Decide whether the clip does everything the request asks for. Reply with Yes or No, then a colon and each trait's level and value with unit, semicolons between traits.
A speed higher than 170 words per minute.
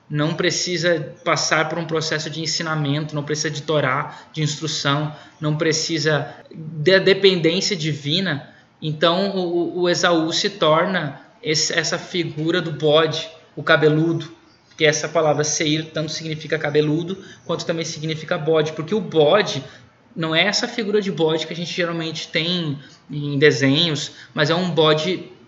No: average, 150 wpm